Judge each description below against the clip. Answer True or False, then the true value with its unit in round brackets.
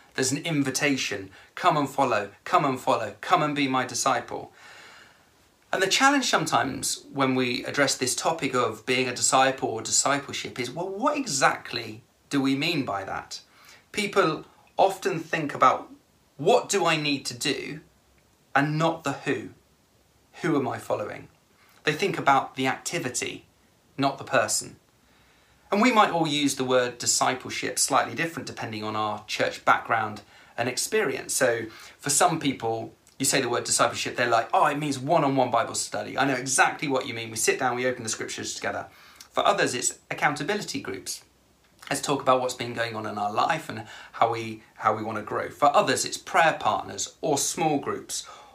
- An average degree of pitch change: True (3.6 semitones)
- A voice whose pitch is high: False (135 Hz)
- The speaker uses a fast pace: False (175 wpm)